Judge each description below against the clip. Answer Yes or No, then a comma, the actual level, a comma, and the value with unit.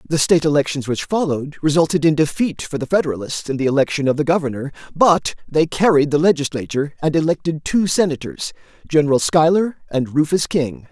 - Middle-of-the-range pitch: Yes, medium, 150 Hz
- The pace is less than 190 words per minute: Yes, average, 165 wpm